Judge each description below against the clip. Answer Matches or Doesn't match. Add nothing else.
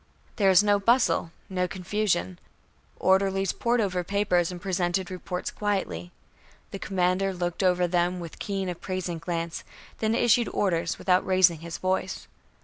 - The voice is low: Doesn't match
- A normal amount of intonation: Doesn't match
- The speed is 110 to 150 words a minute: Matches